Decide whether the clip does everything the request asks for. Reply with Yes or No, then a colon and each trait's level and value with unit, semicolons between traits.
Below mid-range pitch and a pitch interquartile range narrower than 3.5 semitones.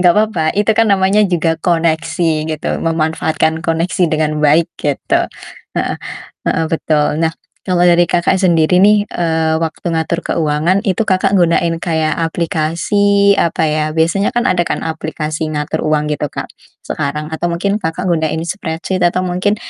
No: medium, 165 Hz; narrow, 2.5 semitones